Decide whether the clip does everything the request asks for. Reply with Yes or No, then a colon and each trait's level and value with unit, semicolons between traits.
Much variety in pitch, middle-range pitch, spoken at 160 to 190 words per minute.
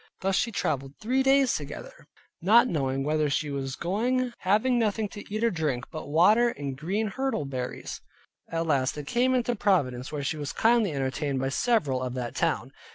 Yes: wide, 8.6 semitones; medium, 165 Hz; average, 185 wpm